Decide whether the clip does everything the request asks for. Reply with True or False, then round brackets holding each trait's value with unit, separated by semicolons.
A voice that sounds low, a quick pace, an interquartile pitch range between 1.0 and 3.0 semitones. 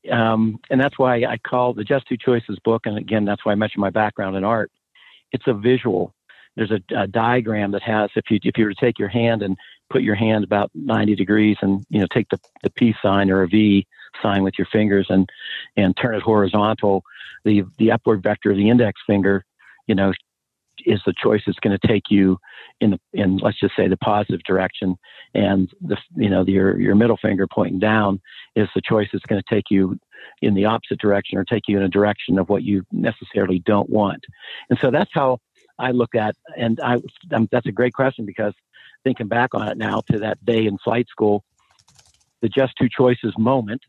True (105 Hz; 215 wpm; 2.6 semitones)